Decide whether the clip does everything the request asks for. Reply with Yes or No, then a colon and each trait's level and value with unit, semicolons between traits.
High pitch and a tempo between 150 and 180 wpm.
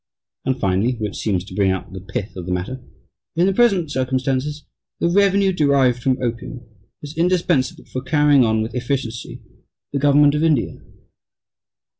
No: low, 130 Hz; average, 160 wpm